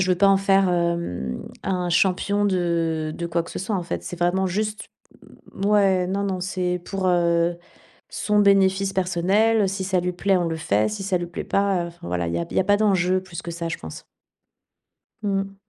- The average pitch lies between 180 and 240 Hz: Yes, medium, 185 Hz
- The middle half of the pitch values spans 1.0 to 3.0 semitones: Yes, narrow, 2.4 semitones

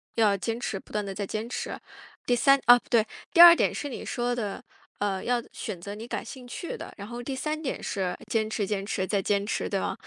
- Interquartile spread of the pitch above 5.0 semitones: No, average, 3.4 semitones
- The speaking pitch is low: No, high, 225 Hz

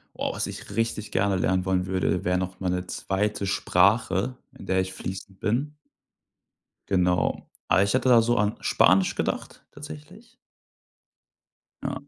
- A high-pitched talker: No, very low, 95 Hz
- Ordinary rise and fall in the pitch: Yes, average, 3.5 semitones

